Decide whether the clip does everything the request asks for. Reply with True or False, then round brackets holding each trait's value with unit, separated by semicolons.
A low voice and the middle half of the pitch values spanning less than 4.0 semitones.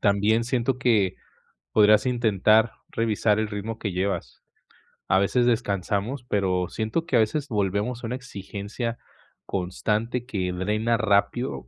True (110 Hz; 2.9 semitones)